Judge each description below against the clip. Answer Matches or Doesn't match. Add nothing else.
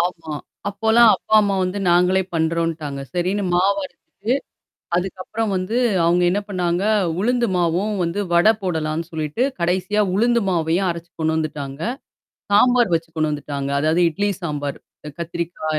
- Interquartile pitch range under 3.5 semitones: Doesn't match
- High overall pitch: Doesn't match